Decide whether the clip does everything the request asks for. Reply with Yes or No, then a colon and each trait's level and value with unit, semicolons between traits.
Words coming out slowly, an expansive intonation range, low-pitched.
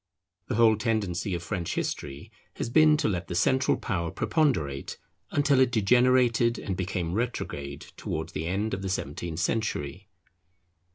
No: average, 150 wpm; wide, 6.1 semitones; low, 100 Hz